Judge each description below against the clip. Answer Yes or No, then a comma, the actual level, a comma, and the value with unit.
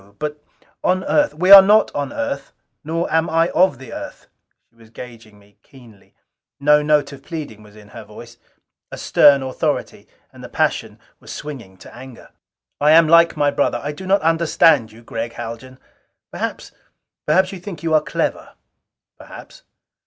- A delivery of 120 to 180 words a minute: Yes, average, 170 wpm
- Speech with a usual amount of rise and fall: No, wide, 5.7 semitones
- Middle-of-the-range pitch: Yes, medium, 150 Hz